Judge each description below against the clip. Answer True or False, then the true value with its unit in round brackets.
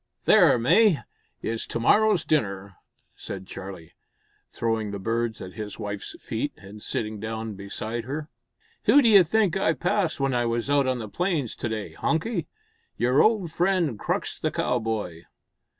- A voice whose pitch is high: False (120 Hz)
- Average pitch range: False (7.8 semitones)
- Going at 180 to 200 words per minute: False (155 wpm)